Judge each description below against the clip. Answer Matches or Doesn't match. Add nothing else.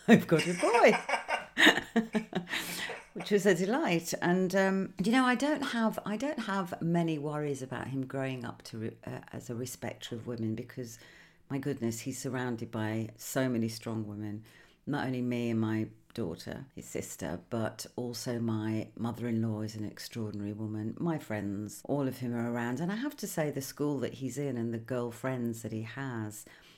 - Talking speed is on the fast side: Doesn't match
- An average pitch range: Doesn't match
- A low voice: Matches